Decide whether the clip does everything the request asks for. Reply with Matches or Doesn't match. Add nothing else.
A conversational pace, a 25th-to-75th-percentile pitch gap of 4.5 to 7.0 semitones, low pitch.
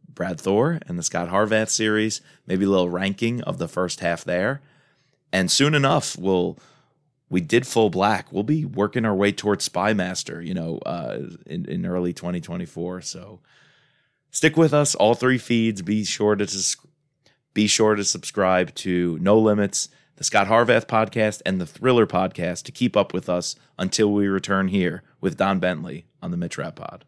Matches